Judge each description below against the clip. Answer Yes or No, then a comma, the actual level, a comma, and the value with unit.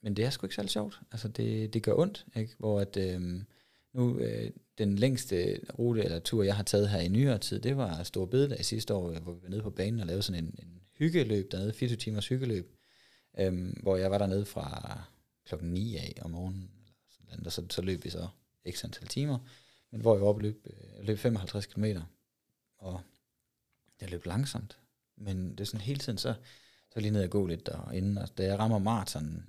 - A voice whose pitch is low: Yes, low, 105 Hz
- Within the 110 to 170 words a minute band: No, fast, 225 wpm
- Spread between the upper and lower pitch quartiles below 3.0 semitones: No, average, 3.6 semitones